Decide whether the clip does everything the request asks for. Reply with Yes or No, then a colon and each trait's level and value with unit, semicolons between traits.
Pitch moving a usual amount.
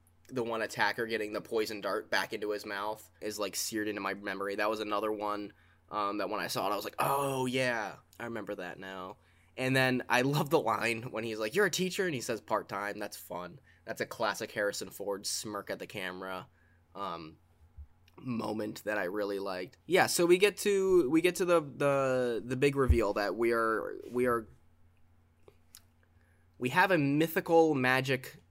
No: wide, 6.2 semitones